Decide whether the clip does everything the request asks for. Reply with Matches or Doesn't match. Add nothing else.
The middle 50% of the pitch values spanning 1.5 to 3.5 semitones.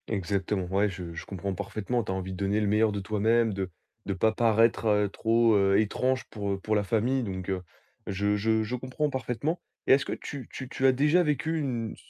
Doesn't match